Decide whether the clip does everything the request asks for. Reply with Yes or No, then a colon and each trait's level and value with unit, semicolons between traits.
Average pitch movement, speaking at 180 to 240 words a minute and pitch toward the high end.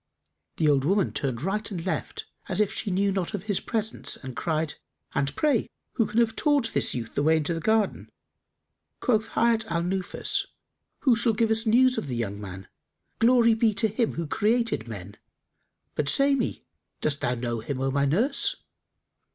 No: wide, 8.1 semitones; average, 185 wpm; high, 195 Hz